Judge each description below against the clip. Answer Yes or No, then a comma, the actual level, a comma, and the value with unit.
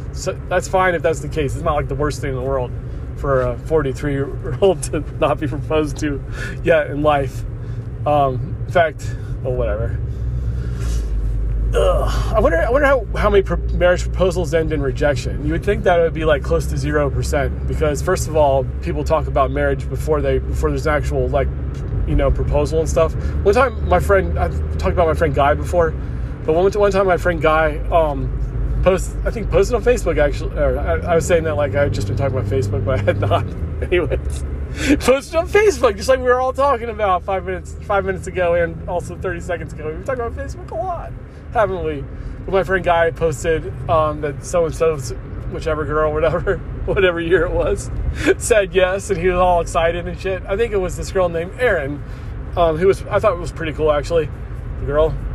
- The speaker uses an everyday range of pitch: No, wide, 7.7 semitones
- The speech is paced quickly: Yes, fast, 215 wpm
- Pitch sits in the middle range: Yes, medium, 150 Hz